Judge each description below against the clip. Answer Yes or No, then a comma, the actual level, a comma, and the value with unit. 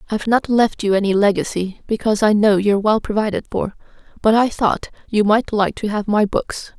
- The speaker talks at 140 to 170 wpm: No, fast, 205 wpm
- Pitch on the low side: No, high, 210 Hz